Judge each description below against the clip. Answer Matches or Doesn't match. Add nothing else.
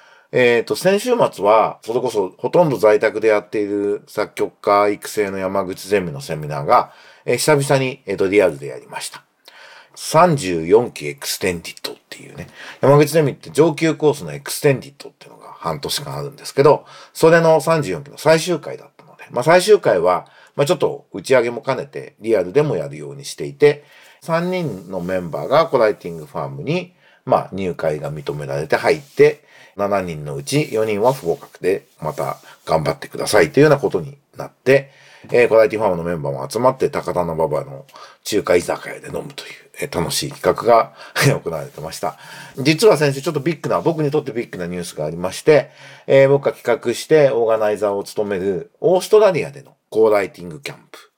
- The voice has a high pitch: Doesn't match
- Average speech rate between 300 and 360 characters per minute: Doesn't match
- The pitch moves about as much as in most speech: Doesn't match